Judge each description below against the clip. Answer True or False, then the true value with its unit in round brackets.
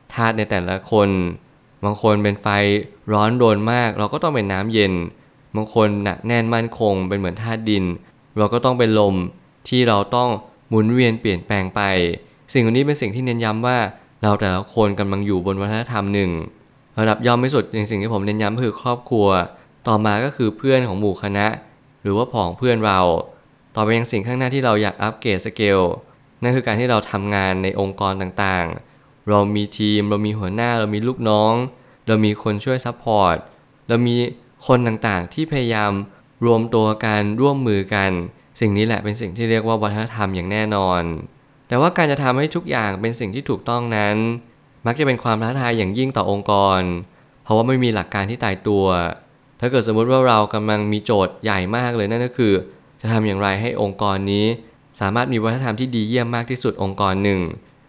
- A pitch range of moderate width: True (3.2 semitones)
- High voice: False (110 Hz)